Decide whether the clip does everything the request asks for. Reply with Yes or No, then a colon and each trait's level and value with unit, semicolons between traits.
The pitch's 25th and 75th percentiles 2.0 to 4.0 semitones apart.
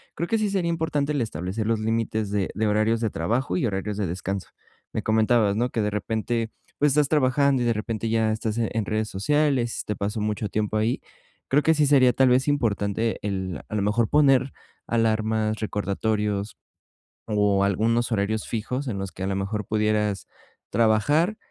Yes: average, 3.0 semitones